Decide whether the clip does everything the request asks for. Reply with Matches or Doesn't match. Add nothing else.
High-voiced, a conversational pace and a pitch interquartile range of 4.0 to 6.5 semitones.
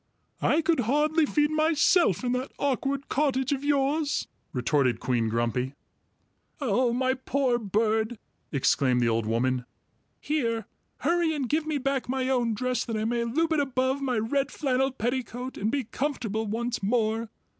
Matches